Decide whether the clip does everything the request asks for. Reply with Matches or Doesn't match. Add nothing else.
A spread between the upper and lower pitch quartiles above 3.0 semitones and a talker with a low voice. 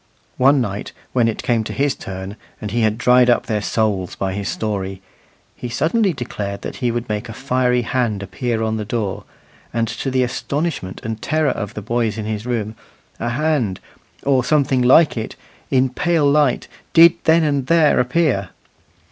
Matches